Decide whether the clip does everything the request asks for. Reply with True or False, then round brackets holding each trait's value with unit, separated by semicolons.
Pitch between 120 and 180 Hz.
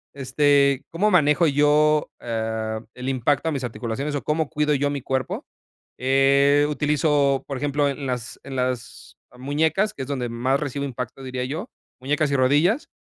True (140 Hz)